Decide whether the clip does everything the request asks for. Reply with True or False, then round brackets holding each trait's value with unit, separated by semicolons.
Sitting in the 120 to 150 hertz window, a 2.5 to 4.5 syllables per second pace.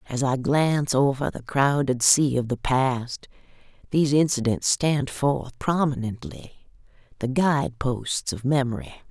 True (135 Hz; 4.1 syllables/s)